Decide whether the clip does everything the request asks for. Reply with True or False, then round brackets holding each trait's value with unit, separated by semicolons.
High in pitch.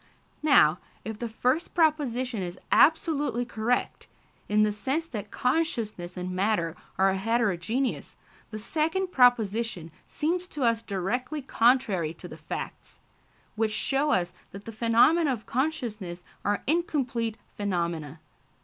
True (230 Hz)